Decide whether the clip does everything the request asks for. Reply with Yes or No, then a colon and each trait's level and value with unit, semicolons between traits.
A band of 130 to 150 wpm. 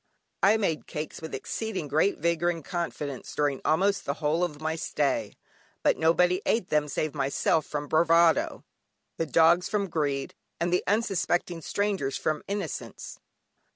Yes: average, 145 wpm